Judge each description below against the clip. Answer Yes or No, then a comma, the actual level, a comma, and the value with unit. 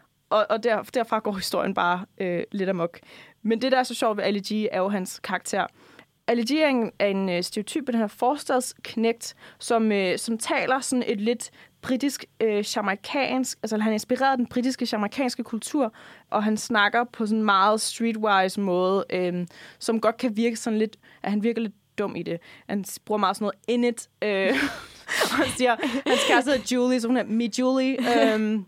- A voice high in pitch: Yes, high, 225 Hz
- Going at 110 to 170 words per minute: No, average, 190 wpm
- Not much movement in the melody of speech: No, average, 3.5 semitones